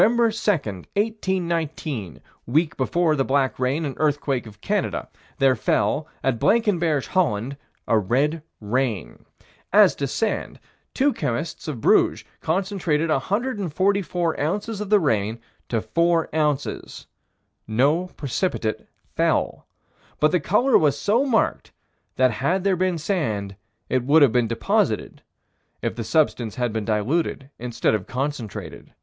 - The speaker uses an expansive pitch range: Yes, wide, 7.1 semitones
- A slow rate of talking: Yes, slow, 130 wpm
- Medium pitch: Yes, medium, 150 Hz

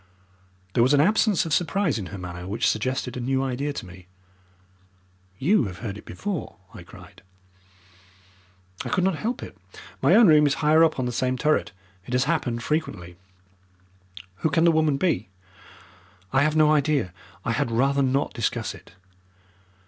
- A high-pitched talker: No, medium, 140 Hz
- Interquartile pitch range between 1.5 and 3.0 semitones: No, average, 5.2 semitones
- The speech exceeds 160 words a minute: Yes, average, 170 wpm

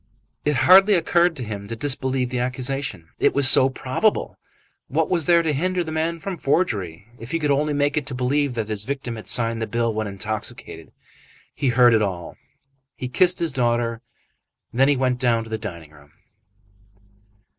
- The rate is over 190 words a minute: No, average, 180 wpm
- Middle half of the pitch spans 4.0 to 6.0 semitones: Yes, average, 4.7 semitones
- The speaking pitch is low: Yes, low, 130 Hz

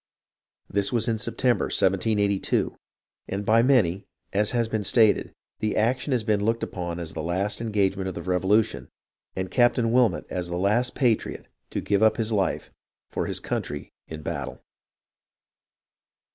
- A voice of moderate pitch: No, low, 105 Hz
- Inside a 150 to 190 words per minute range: Yes, average, 155 wpm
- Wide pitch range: No, average, 3.4 semitones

